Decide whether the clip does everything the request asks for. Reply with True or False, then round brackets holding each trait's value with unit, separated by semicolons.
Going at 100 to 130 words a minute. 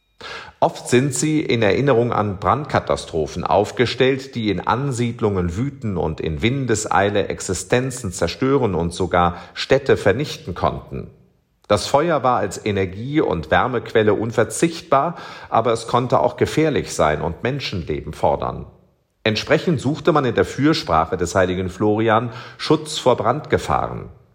True (125 wpm)